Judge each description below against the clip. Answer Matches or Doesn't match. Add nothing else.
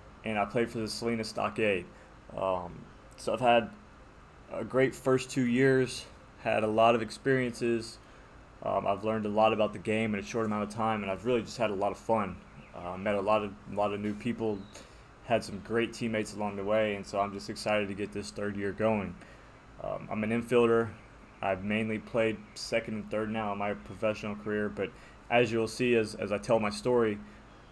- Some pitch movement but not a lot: Doesn't match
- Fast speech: Matches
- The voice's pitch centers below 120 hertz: Matches